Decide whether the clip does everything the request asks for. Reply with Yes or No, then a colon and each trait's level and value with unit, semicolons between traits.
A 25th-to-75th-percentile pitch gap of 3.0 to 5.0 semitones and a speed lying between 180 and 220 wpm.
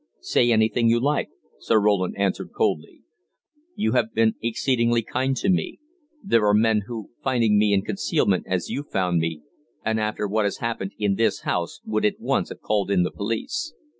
No: narrow, 2.6 semitones; average, 185 wpm